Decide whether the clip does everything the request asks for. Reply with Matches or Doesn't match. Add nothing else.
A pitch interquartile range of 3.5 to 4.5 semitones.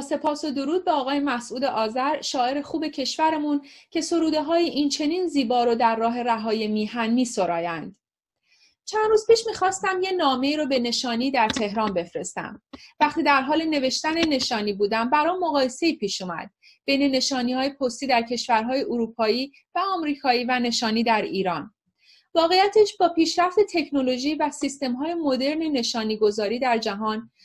Doesn't match